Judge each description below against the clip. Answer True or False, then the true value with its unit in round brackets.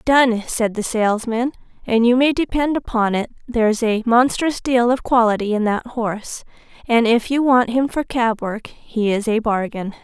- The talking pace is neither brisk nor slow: True (180 wpm)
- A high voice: True (235 Hz)